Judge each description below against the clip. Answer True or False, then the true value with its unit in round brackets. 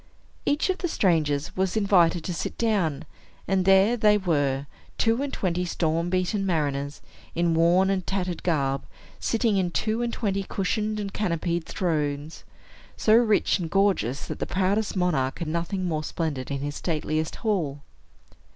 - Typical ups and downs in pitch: True (4.2 semitones)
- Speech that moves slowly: False (160 wpm)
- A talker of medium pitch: True (180 Hz)